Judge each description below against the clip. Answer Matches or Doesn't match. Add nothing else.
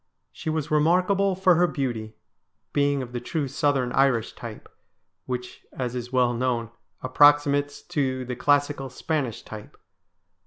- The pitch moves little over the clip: Doesn't match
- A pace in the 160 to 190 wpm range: Doesn't match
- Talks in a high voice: Doesn't match